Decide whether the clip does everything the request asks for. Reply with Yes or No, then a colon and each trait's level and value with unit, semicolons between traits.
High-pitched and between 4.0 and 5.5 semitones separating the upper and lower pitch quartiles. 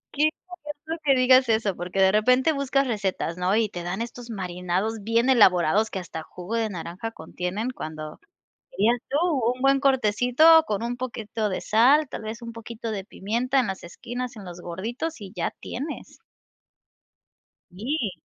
Yes: high, 225 Hz; average, 5.1 semitones